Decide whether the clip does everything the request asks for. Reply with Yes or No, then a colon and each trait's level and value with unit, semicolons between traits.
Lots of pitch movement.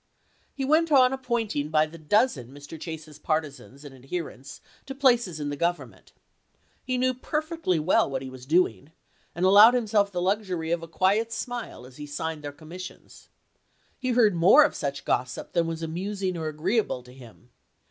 Yes: wide, 7.2 semitones